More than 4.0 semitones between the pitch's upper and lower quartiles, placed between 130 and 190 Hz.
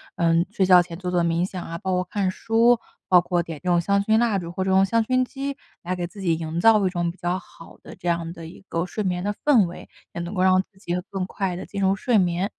No: narrow, 2.6 semitones; medium, 185 Hz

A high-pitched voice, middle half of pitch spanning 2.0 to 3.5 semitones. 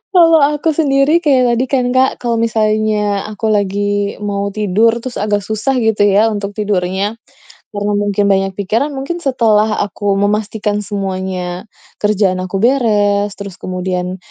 Yes: high, 210 Hz; narrow, 2.6 semitones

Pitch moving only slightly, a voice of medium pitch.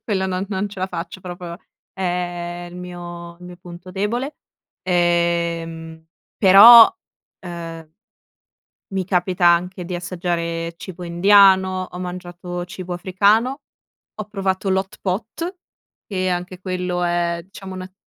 Yes: narrow, 1.7 semitones; medium, 180 Hz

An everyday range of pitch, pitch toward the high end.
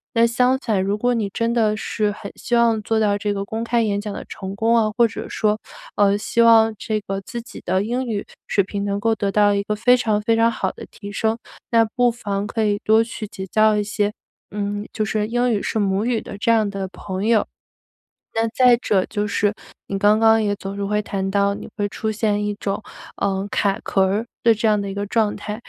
No: narrow, 2.0 semitones; high, 210 Hz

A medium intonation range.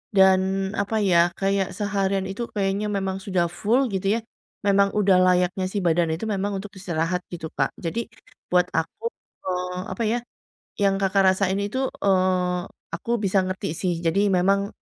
No: narrow, 1.7 semitones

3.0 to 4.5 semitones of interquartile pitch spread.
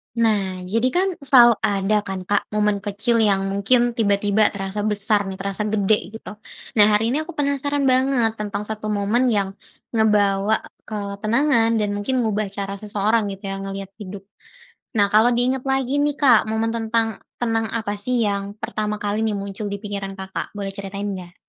No: narrow, 2.5 semitones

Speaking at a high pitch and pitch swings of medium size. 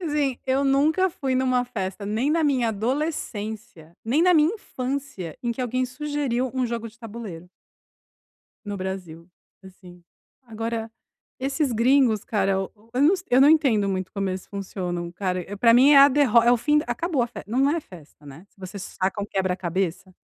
No: high, 230 Hz; wide, 6.0 semitones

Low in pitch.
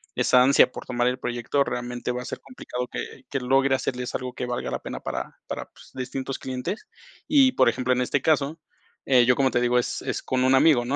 Yes: low, 130 Hz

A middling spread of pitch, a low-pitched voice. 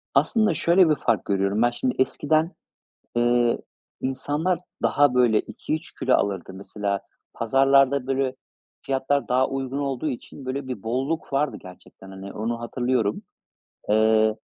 Yes: average, 4.1 semitones; low, 130 Hz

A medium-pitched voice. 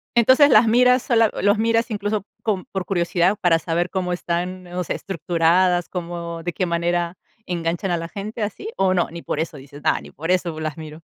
Yes: medium, 180 Hz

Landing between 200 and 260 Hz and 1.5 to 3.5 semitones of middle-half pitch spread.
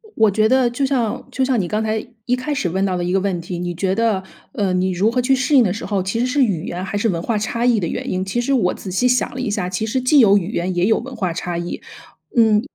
No: high, 210 Hz; average, 4.7 semitones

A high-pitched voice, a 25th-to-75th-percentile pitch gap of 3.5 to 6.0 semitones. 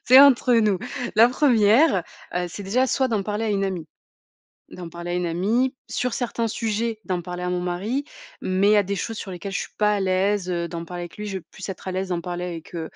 Yes: high, 195 Hz; average, 4.1 semitones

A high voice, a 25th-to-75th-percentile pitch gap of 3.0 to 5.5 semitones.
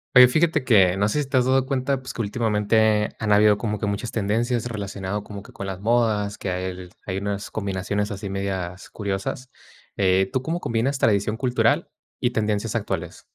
No: low, 105 Hz; average, 3.4 semitones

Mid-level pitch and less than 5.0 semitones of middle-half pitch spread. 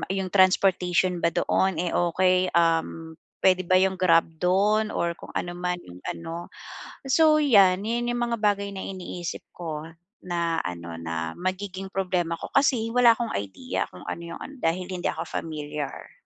Yes: medium, 180 Hz; average, 2.8 semitones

